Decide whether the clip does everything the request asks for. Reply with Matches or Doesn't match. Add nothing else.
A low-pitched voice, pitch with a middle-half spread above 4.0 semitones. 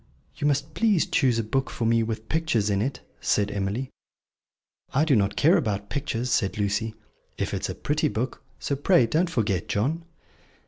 Matches